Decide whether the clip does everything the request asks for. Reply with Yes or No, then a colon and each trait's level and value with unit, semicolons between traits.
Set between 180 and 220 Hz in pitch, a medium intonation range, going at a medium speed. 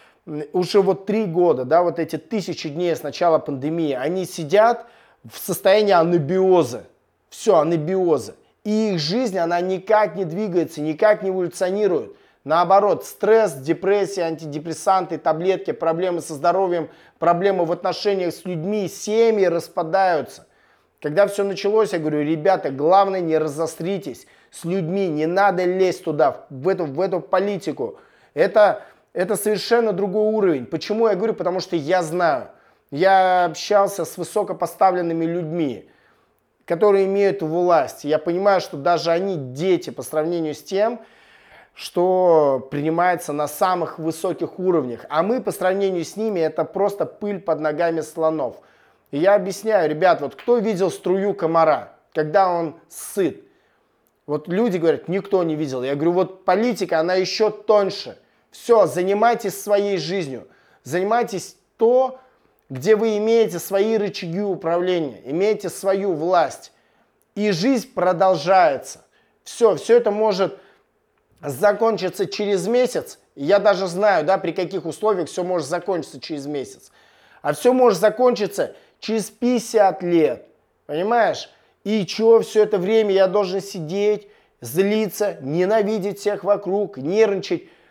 Yes: medium, 185 Hz; average, 3.6 semitones; average, 135 wpm